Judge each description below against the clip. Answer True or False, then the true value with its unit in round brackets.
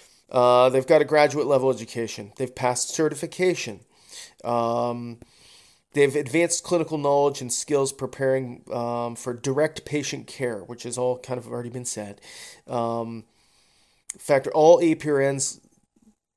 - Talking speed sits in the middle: False (130 wpm)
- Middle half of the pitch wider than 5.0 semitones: False (3.7 semitones)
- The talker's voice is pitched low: True (130 Hz)